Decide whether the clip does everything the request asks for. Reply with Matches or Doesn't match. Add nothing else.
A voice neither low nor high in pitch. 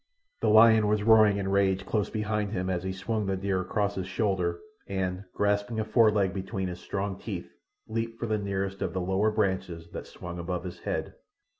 Doesn't match